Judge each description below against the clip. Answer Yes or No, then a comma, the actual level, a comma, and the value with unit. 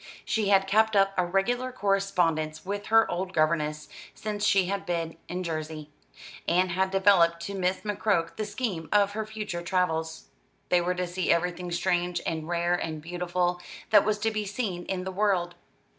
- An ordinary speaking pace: Yes, average, 175 wpm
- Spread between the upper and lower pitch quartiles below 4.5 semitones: Yes, average, 2.8 semitones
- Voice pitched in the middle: Yes, medium, 180 Hz